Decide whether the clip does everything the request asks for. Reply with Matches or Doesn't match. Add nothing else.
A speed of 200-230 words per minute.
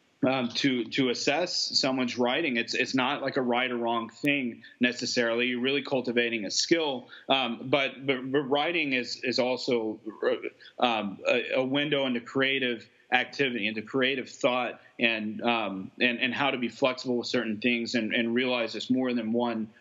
Doesn't match